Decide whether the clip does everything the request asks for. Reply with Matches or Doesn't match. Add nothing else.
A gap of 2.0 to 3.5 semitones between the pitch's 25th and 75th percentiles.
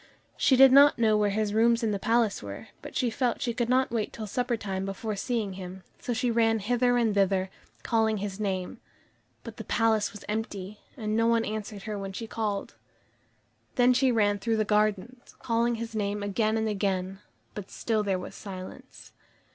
Matches